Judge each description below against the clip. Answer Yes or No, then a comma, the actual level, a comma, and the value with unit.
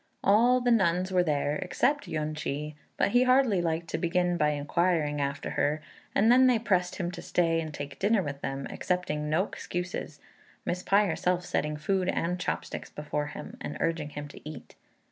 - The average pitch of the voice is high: No, medium, 170 Hz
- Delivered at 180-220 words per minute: Yes, average, 190 wpm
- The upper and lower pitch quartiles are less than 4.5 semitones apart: Yes, average, 4.1 semitones